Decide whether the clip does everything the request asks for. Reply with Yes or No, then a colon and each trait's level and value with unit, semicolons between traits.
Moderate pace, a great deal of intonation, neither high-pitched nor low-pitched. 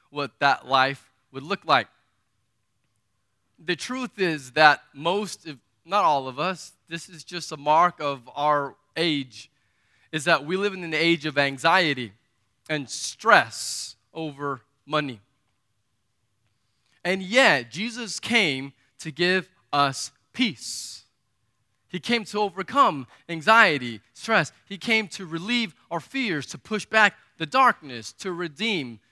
No: slow, 130 wpm; wide, 7.0 semitones; medium, 150 Hz